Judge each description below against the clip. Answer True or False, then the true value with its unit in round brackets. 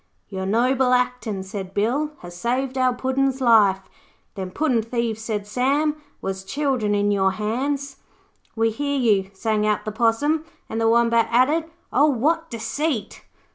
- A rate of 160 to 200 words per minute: False (150 wpm)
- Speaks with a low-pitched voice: False (235 Hz)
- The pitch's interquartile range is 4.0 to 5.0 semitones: True (4.3 semitones)